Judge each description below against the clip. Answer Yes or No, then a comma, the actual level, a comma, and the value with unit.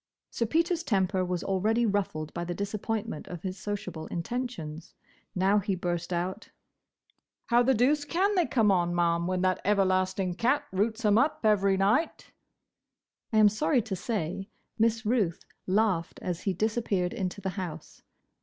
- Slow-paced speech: No, average, 155 wpm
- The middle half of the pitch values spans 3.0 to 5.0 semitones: Yes, average, 3.8 semitones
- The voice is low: No, high, 200 Hz